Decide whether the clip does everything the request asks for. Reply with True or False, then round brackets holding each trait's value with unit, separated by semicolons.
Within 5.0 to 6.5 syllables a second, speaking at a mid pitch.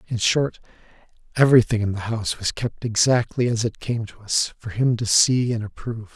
False (5.4 syllables/s; 110 Hz)